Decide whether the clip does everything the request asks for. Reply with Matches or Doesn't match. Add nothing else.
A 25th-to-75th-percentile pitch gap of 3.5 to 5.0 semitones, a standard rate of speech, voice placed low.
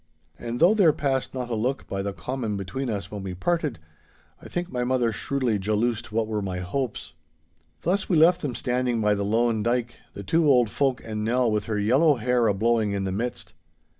Doesn't match